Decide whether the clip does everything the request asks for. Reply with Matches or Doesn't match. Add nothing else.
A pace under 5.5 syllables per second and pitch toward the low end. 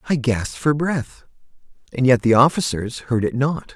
Matches